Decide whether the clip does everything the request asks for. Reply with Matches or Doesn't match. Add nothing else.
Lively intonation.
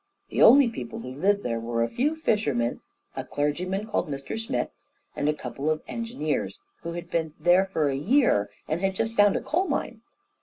Matches